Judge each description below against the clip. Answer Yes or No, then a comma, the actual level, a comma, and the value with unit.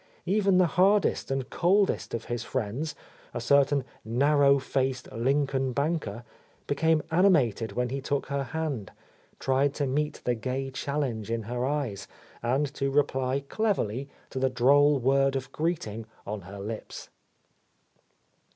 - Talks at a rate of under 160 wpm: Yes, average, 140 wpm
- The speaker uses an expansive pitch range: No, average, 3.3 semitones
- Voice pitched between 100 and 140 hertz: Yes, low, 135 Hz